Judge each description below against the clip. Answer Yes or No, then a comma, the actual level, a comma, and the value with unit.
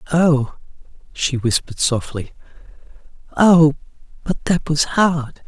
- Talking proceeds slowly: Yes, slow, 100 wpm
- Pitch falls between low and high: Yes, medium, 145 Hz